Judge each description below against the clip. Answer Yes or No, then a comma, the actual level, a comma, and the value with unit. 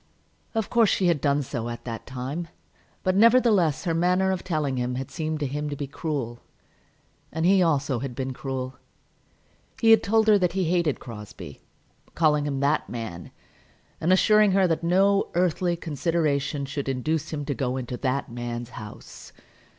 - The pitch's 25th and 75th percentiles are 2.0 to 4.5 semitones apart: No, wide, 5.5 semitones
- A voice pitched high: No, medium, 150 Hz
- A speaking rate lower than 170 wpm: No, average, 175 wpm